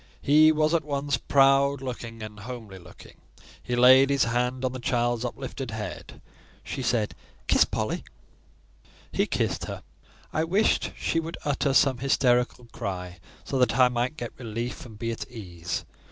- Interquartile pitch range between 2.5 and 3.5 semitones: Yes, average, 3.2 semitones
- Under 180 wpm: Yes, average, 155 wpm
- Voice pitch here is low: Yes, low, 125 Hz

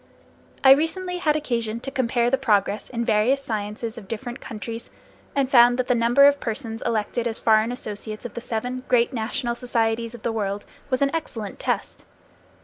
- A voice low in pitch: No, high, 235 Hz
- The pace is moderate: Yes, average, 180 wpm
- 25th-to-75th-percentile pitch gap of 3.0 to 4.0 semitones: No, narrow, 2.6 semitones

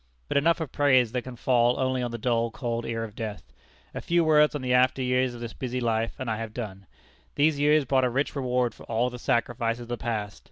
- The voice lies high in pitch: No, low, 125 Hz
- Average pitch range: No, narrow, 2.1 semitones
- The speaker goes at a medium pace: No, fast, 245 wpm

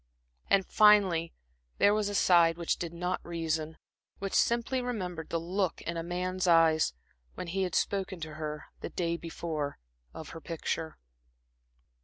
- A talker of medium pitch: Yes, medium, 170 Hz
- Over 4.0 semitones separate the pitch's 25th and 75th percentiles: No, average, 2.7 semitones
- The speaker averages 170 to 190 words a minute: No, average, 155 wpm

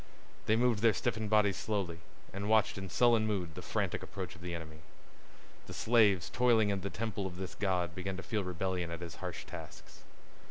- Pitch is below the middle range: Yes, very low, 95 Hz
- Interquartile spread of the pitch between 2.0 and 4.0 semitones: Yes, average, 3.4 semitones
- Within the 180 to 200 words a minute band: Yes, average, 195 wpm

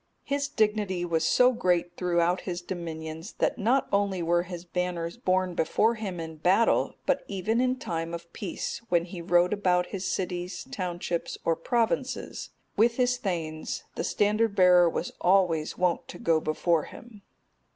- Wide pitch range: No, average, 3.5 semitones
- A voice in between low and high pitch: Yes, medium, 180 Hz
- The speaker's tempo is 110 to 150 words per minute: No, average, 160 wpm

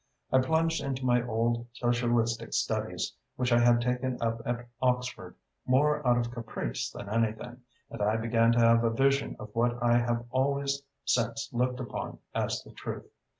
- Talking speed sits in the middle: Yes, average, 170 wpm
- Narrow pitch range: Yes, narrow, 1.6 semitones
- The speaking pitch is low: Yes, low, 120 Hz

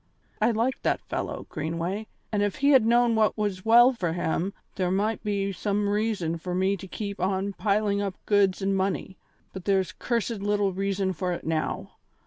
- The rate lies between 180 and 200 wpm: Yes, average, 185 wpm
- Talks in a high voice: Yes, high, 200 Hz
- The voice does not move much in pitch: Yes, narrow, 2.3 semitones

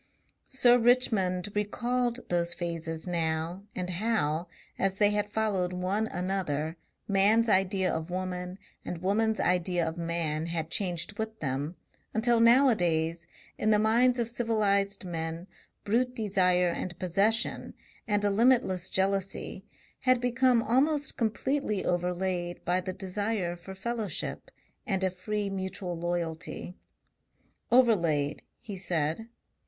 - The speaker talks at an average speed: No, slow, 125 wpm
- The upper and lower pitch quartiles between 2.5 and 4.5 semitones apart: Yes, average, 4.1 semitones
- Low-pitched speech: No, high, 190 Hz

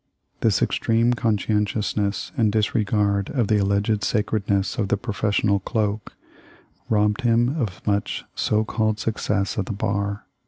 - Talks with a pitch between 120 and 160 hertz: No, low, 105 Hz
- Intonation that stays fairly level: Yes, narrow, 1.6 semitones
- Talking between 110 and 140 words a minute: Yes, slow, 135 wpm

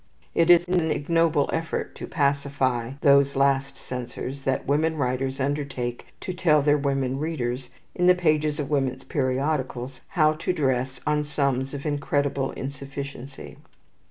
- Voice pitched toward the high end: No, medium, 140 Hz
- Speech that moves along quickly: No, average, 145 wpm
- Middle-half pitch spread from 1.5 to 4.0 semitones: Yes, narrow, 2.4 semitones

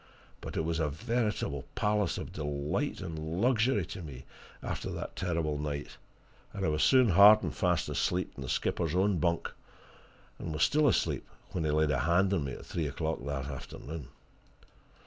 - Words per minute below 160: No, average, 180 wpm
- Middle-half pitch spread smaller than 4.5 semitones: No, average, 5.1 semitones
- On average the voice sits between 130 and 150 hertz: No, very low, 85 Hz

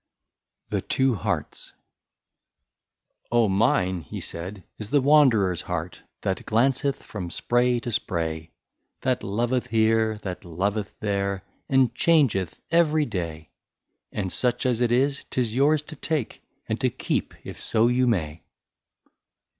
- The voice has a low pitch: Yes, low, 110 Hz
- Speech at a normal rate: Yes, average, 145 wpm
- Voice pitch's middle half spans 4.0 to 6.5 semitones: Yes, wide, 5.4 semitones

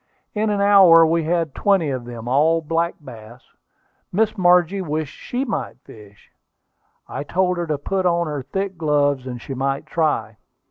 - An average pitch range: Yes, average, 4.8 semitones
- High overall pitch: No, medium, 165 Hz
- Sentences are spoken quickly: No, average, 170 wpm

